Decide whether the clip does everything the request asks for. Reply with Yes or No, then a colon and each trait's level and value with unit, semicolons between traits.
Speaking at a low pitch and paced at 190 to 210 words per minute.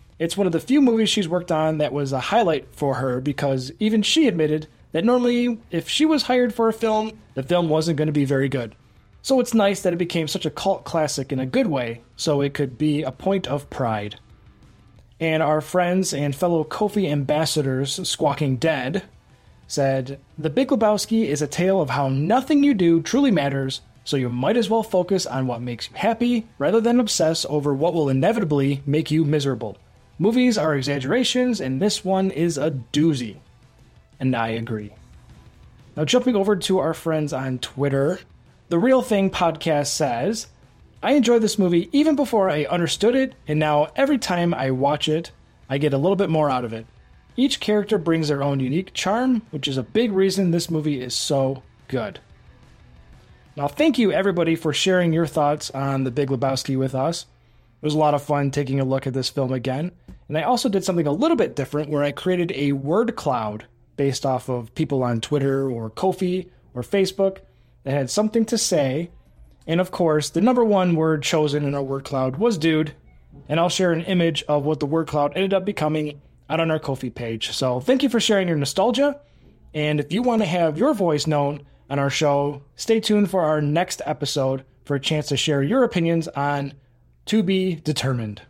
No: medium, 155 Hz; average, 200 wpm